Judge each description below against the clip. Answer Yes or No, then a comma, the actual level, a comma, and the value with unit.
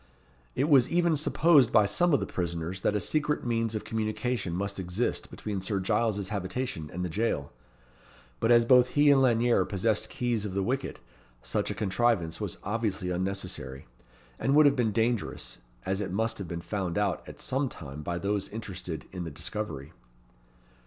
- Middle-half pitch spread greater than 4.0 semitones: Yes, average, 4.8 semitones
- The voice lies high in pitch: No, low, 105 Hz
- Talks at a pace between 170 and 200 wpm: Yes, average, 180 wpm